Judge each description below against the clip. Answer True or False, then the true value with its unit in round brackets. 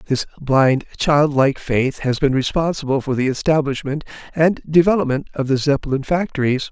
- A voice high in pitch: False (140 Hz)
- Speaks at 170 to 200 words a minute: False (150 wpm)